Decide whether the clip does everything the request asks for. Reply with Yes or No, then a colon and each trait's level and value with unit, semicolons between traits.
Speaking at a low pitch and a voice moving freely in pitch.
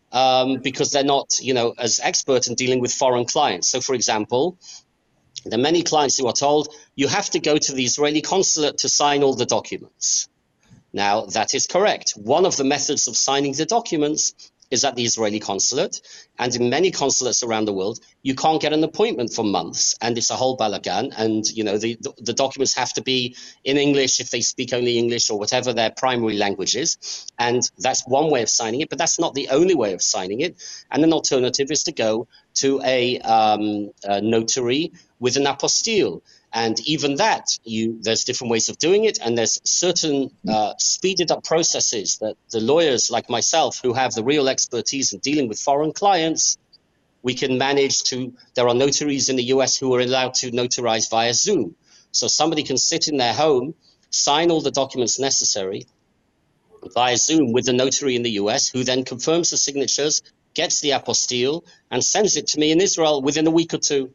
No: low, 130 Hz; average, 3.6 semitones